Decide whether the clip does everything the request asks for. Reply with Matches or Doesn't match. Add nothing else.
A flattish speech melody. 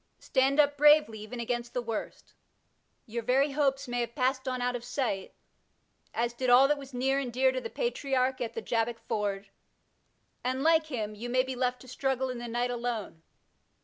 Matches